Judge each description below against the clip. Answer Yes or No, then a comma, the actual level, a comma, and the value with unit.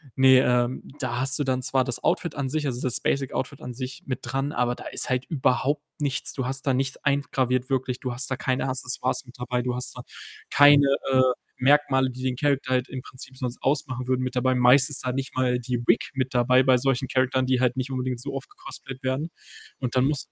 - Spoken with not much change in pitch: Yes, narrow, 1.2 semitones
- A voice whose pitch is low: Yes, low, 130 Hz